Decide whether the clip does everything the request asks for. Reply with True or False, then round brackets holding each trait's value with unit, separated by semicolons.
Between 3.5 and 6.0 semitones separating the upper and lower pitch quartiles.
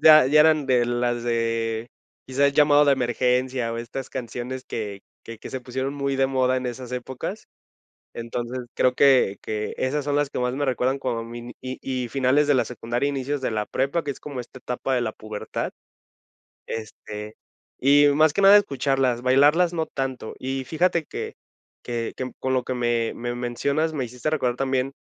False (2.6 semitones)